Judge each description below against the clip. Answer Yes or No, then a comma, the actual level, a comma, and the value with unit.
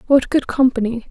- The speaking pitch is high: Yes, very high, 250 Hz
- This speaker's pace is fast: No, average, 160 wpm